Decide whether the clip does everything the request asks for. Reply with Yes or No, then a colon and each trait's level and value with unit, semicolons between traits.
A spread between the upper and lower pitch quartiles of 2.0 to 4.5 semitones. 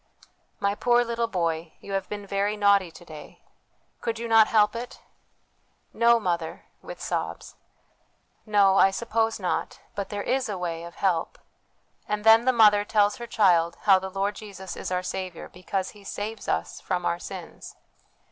Yes: average, 3.3 semitones